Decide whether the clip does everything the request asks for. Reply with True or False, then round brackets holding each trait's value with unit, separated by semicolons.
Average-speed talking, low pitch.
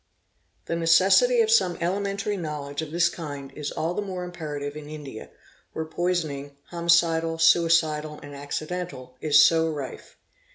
False (155 wpm; 165 Hz)